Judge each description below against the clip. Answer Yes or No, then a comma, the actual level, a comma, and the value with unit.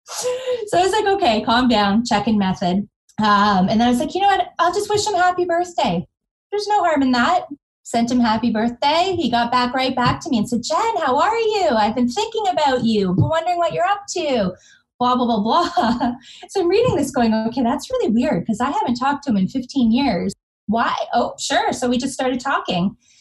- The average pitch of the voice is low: No, very high, 255 Hz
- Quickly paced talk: Yes, fast, 230 wpm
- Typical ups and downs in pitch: No, wide, 7.7 semitones